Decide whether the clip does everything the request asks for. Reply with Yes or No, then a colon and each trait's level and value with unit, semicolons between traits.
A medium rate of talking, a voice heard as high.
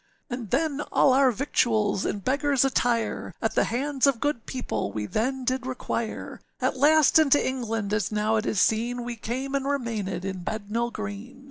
Yes: average, 175 wpm; high, 245 Hz